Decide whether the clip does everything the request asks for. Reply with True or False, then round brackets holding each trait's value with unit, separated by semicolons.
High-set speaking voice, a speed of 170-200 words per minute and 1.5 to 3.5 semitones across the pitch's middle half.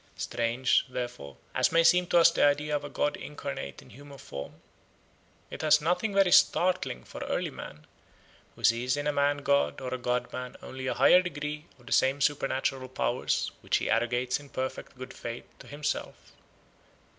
False (140 Hz; 180 wpm; 3.1 semitones)